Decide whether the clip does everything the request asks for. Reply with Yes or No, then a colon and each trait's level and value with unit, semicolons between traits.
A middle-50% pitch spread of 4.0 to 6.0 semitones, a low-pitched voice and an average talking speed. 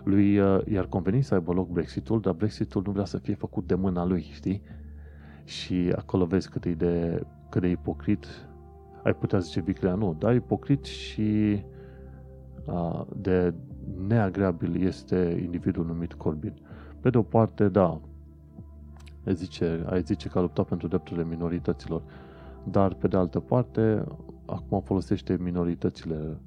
Yes: average, 4.4 semitones; very low, 90 Hz; average, 145 wpm